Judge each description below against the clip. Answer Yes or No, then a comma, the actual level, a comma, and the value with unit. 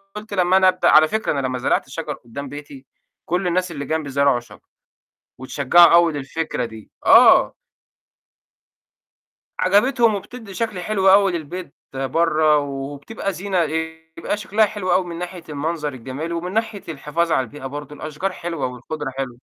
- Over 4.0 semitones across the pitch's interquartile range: Yes, average, 4.7 semitones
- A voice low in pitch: No, medium, 160 Hz